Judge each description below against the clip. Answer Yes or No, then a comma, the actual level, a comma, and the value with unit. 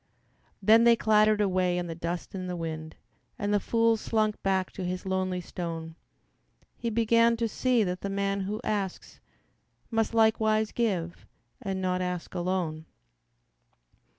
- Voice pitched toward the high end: Yes, high, 195 Hz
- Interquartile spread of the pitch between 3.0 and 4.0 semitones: Yes, average, 3.4 semitones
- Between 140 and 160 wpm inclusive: Yes, average, 150 wpm